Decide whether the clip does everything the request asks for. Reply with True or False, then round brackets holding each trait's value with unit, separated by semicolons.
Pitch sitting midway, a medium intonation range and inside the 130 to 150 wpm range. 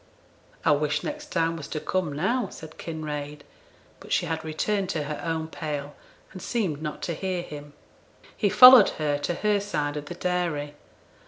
False (160 Hz; 4.0 semitones; 175 wpm)